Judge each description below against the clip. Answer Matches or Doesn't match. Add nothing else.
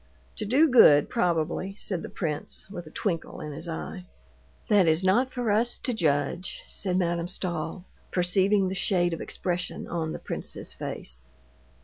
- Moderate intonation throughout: Matches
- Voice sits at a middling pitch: Matches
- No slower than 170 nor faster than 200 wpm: Doesn't match